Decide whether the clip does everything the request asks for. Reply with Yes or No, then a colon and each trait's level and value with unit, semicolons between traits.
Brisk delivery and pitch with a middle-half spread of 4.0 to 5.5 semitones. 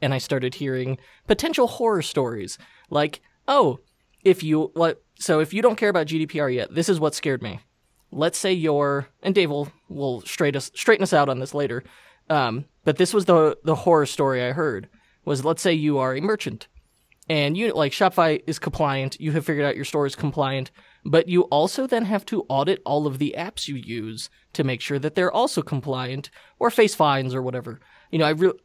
Yes: fast, 210 wpm; average, 4.6 semitones